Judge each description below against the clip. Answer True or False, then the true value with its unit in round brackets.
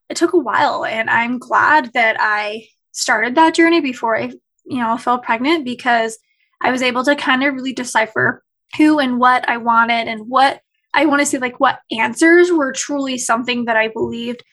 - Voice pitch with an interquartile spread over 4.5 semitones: False (4.2 semitones)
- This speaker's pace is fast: False (190 wpm)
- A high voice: True (255 Hz)